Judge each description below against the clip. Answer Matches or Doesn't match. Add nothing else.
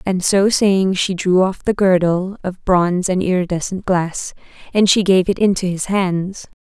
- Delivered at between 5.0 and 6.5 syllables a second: Doesn't match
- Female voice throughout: Matches